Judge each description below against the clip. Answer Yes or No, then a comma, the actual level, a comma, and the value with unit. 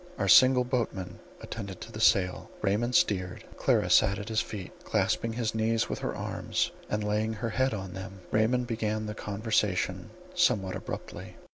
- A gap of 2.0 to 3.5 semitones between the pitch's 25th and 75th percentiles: Yes, average, 2.8 semitones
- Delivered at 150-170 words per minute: Yes, average, 165 wpm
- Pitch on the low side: Yes, low, 110 Hz